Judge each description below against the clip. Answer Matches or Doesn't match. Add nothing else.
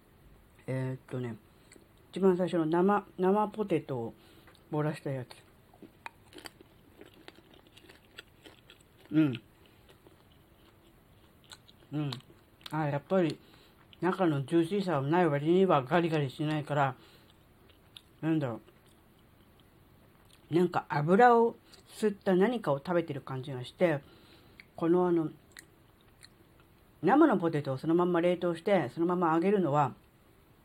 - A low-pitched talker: Doesn't match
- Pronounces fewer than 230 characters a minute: Matches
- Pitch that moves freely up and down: Matches